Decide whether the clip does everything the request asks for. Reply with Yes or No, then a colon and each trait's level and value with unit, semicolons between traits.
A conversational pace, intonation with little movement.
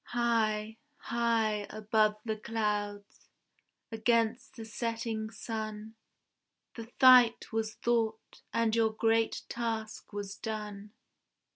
No: slow, 100 wpm; narrow, 1.2 semitones